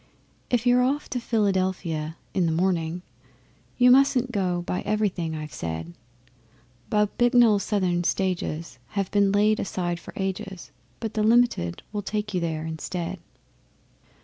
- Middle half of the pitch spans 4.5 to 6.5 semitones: No, average, 4.0 semitones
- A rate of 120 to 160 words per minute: Yes, average, 140 wpm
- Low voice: No, high, 190 Hz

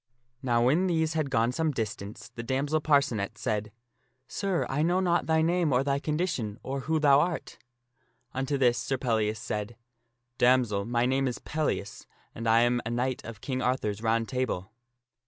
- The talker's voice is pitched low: Yes, low, 130 Hz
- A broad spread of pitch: No, average, 4.4 semitones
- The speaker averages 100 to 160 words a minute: No, average, 185 wpm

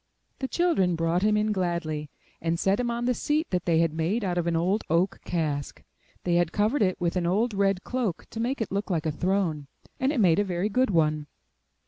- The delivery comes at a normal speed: No, fast, 220 wpm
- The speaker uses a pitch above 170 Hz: Yes, medium, 185 Hz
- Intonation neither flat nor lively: Yes, average, 4.4 semitones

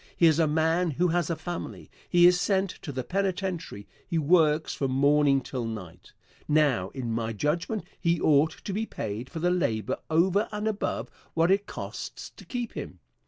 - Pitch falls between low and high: Yes, medium, 160 Hz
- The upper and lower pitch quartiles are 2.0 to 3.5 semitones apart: No, average, 4.7 semitones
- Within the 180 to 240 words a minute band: Yes, average, 185 wpm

